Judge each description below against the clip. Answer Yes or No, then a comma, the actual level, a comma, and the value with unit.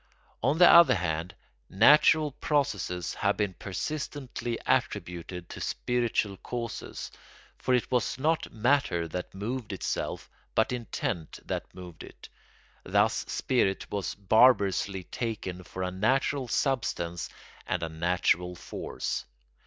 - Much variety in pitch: Yes, wide, 6.1 semitones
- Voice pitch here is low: Yes, low, 105 Hz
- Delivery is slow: Yes, slow, 120 wpm